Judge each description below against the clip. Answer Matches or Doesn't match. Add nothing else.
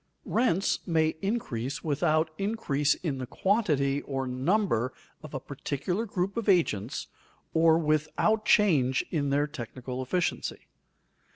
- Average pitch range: Doesn't match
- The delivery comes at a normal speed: Doesn't match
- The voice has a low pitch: Doesn't match